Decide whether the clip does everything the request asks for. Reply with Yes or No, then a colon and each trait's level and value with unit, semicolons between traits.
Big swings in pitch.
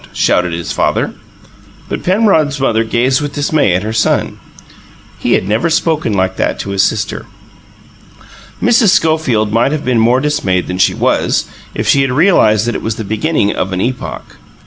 Yes: wide, 6.4 semitones